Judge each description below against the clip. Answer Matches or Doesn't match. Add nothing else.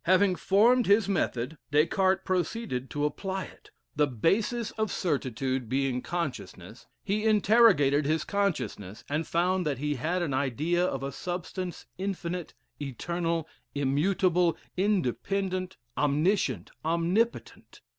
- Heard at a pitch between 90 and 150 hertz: Doesn't match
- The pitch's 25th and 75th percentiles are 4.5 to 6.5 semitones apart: Matches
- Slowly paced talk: Matches